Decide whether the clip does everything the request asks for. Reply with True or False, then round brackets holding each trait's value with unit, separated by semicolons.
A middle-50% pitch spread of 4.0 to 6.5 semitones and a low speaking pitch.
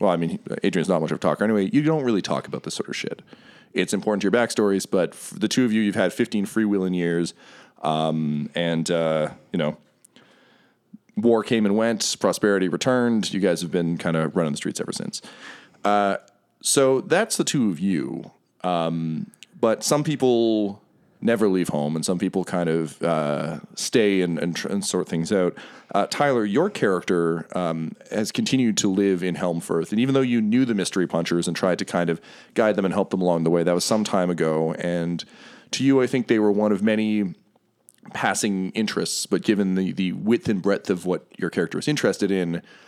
True (4.6 semitones; 95 Hz)